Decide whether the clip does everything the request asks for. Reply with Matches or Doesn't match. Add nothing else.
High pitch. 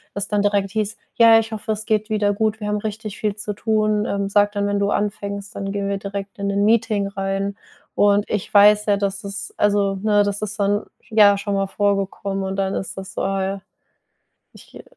Matches